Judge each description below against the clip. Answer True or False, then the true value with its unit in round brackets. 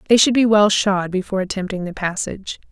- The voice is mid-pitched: False (200 Hz)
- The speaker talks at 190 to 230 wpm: True (200 wpm)